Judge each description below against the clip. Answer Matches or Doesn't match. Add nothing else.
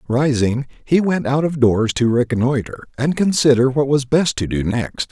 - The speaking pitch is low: Matches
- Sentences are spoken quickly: Doesn't match